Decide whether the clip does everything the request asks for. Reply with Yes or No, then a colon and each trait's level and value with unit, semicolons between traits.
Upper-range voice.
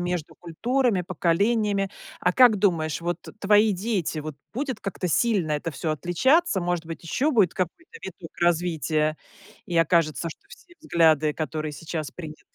No: medium, 175 Hz